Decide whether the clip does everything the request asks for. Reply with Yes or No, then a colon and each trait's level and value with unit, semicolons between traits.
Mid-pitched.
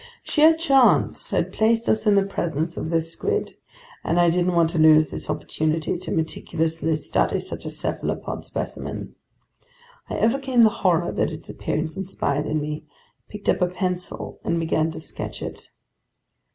Yes: medium, 170 Hz